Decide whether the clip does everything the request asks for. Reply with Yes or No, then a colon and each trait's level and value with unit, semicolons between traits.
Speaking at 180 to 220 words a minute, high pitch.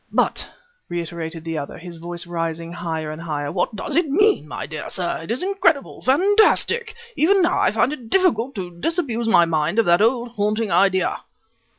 Yes: average, 185 wpm; high, 200 Hz